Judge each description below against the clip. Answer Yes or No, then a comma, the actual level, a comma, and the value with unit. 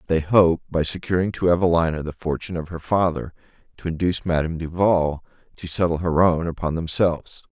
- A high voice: No, very low, 85 Hz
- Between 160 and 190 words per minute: Yes, average, 165 wpm